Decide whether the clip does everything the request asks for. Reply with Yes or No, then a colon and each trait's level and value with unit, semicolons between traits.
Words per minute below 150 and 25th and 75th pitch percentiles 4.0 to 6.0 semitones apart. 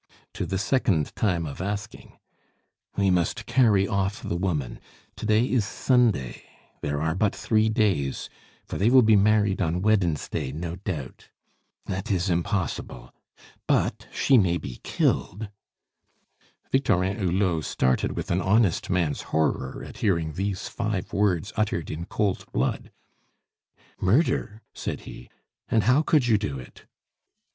Yes: average, 140 wpm; average, 4.3 semitones